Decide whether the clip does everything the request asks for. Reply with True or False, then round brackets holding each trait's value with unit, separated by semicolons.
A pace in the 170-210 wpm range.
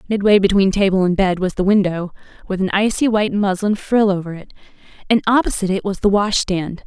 True (200 wpm)